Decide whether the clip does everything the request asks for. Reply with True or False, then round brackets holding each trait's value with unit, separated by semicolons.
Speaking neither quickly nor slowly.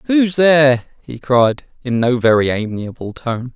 True (150 wpm)